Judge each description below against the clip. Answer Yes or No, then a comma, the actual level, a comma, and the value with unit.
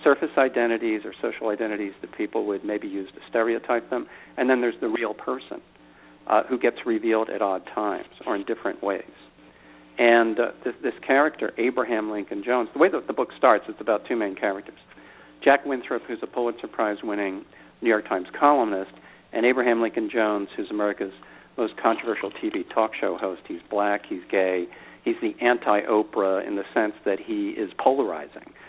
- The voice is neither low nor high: No, low, 115 Hz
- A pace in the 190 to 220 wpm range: No, average, 180 wpm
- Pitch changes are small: No, average, 3.8 semitones